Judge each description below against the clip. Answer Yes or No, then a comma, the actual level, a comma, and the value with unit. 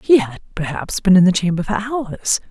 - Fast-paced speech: Yes, fast, 215 wpm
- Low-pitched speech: No, high, 195 Hz